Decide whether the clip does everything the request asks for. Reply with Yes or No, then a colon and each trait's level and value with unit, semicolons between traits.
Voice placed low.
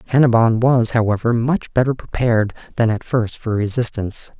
Yes: low, 115 Hz